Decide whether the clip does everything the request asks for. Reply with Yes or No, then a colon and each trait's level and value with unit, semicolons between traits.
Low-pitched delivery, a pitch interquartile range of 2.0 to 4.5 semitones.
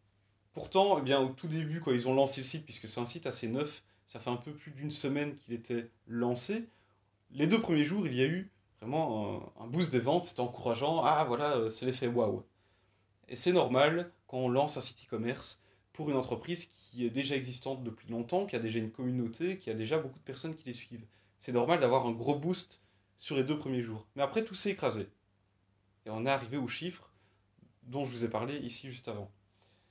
No: low, 125 Hz; average, 5.3 semitones